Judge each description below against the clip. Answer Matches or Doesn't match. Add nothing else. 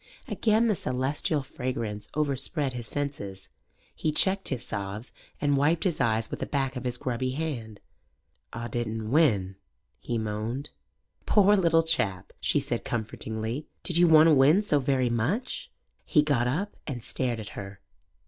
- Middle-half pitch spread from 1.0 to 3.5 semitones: Doesn't match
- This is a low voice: Matches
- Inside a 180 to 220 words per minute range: Doesn't match